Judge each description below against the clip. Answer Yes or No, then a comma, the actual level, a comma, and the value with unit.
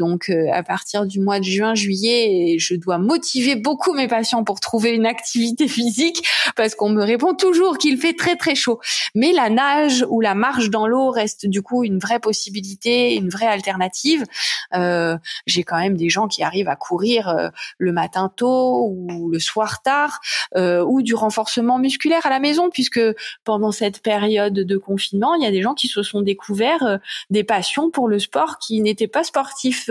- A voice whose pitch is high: Yes, high, 220 Hz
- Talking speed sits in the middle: Yes, average, 195 wpm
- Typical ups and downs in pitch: Yes, average, 4.7 semitones